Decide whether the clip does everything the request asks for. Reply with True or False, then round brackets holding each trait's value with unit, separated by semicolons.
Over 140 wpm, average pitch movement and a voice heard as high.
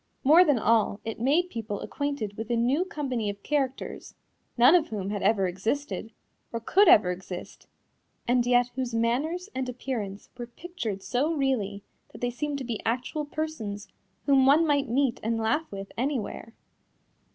True (165 wpm; 4.7 semitones; 245 Hz)